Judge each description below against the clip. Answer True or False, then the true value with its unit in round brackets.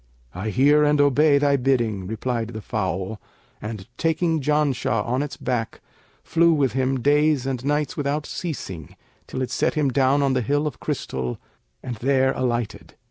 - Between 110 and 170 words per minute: True (165 wpm)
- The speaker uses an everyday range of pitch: True (4.0 semitones)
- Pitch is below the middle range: True (130 Hz)